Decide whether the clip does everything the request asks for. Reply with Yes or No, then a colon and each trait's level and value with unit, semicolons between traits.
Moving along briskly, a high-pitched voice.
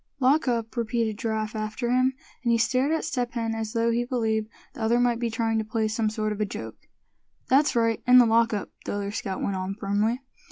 Yes: fast, 230 wpm; high, 230 Hz